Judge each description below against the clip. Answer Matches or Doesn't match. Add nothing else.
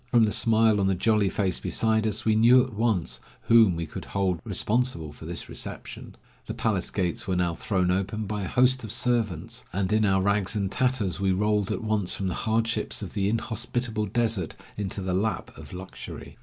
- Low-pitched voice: Matches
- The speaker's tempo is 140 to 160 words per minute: Doesn't match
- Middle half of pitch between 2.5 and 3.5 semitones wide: Matches